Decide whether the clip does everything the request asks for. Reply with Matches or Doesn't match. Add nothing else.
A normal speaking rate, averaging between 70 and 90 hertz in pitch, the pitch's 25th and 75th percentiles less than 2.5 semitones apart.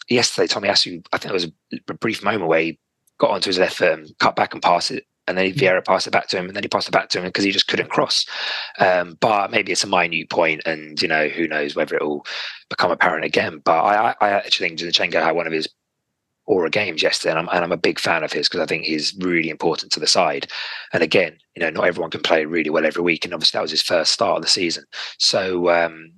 Doesn't match